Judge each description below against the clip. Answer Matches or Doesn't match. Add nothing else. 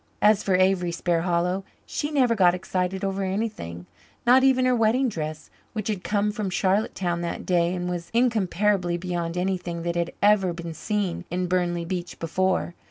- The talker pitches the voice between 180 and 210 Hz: Matches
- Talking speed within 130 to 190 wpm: Matches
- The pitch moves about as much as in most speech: Matches